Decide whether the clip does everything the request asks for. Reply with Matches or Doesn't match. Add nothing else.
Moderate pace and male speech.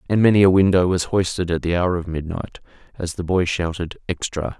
Doesn't match